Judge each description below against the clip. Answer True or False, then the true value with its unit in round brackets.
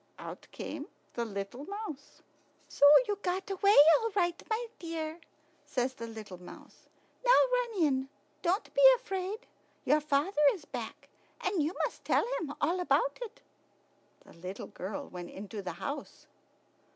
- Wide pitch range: True (8.5 semitones)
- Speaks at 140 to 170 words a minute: True (150 wpm)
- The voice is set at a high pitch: True (315 Hz)